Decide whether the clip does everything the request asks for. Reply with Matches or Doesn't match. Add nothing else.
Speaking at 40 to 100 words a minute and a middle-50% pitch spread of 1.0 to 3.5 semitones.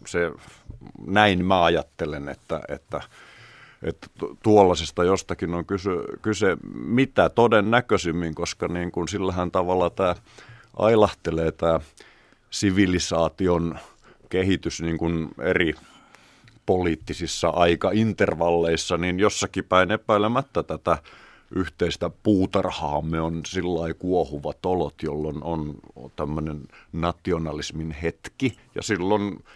Matches